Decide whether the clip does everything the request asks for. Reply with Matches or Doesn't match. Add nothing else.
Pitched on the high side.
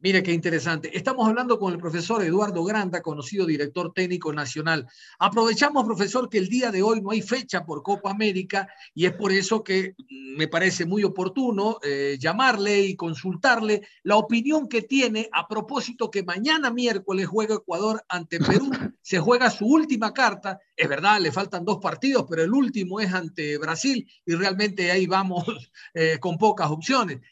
Matches